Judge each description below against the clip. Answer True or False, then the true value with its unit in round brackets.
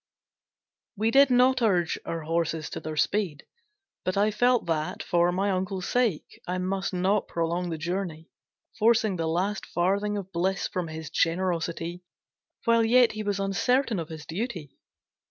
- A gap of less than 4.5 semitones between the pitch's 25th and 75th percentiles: True (4.1 semitones)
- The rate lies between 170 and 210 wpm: False (155 wpm)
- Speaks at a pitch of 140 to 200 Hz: True (185 Hz)